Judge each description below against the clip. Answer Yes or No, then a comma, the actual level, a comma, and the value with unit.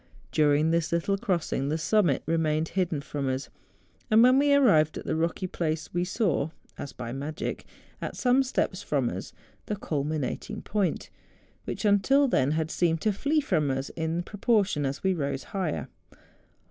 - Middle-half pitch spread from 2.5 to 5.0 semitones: No, wide, 5.4 semitones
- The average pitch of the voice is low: No, medium, 165 Hz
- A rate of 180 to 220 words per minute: No, average, 165 wpm